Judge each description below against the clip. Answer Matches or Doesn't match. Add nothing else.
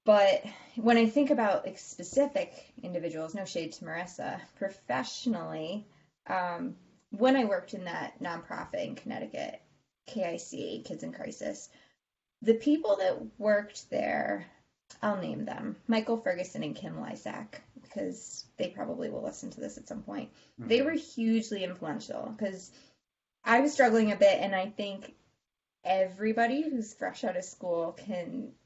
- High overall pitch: Matches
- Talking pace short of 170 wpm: Matches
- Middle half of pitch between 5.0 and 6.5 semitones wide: Matches